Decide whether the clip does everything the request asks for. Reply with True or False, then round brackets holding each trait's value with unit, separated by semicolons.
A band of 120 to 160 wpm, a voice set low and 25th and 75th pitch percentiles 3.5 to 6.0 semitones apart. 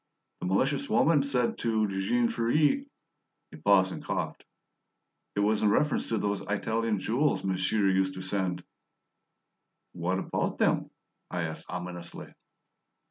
True (140 wpm; 100 Hz; 3.9 semitones)